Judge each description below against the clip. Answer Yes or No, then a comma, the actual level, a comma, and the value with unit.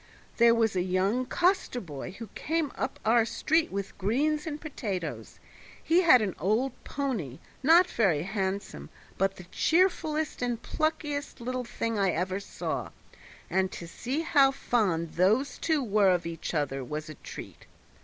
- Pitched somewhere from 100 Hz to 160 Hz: No, high, 230 Hz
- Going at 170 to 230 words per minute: No, average, 155 wpm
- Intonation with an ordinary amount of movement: No, wide, 7.4 semitones